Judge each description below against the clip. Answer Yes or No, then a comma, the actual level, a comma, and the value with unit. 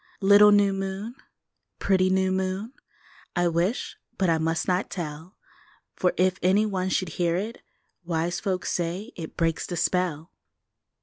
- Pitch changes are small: Yes, narrow, 2.2 semitones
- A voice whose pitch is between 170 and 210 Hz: Yes, medium, 185 Hz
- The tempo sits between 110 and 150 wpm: Yes, average, 145 wpm